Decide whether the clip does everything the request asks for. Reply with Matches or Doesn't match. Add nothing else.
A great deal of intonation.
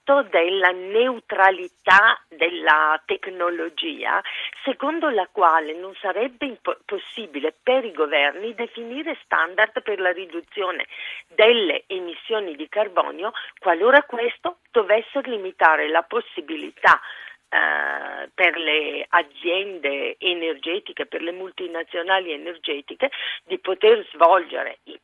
Matches